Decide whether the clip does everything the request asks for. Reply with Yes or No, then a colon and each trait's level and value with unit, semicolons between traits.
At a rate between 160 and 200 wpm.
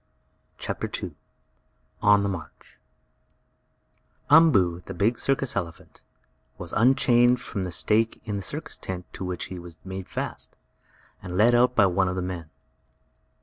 No: average, 145 wpm